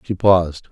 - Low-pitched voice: Yes, very low, 90 Hz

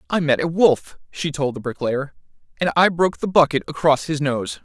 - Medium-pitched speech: Yes, medium, 150 Hz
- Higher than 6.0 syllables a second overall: No, 5.3 syllables/s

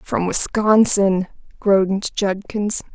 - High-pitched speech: Yes, high, 200 Hz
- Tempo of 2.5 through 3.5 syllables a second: Yes, 3.3 syllables/s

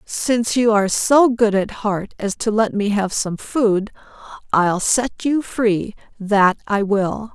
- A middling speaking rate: Yes, average, 170 wpm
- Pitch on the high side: Yes, high, 215 Hz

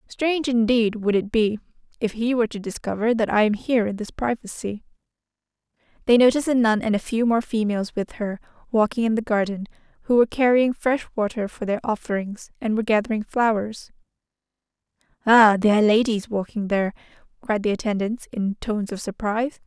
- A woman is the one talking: Yes, female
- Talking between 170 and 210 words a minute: Yes, average, 175 wpm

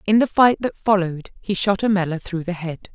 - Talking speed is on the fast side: Yes, fast, 225 wpm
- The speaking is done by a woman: Yes, female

